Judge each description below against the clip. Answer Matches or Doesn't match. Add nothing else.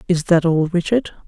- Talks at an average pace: Matches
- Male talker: Doesn't match